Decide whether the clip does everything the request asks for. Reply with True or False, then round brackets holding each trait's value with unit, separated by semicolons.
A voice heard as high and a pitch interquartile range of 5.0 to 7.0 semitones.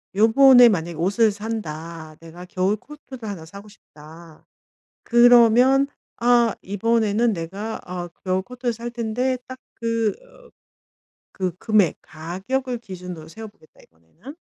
True (215 Hz; 5.3 semitones)